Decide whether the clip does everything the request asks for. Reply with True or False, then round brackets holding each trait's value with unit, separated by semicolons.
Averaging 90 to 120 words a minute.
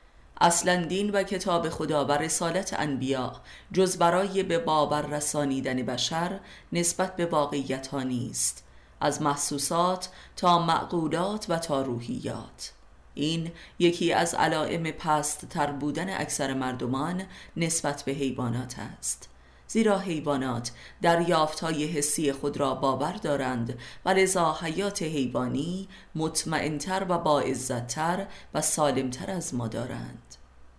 True (115 wpm)